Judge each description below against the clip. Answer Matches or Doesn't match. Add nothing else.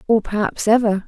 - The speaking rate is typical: Matches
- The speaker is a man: Doesn't match